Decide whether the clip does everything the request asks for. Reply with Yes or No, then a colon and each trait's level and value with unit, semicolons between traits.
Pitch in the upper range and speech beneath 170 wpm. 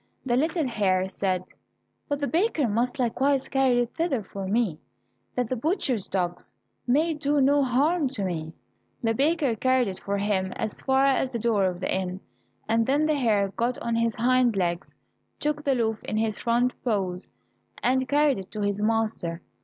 No: high, 235 Hz; average, 185 wpm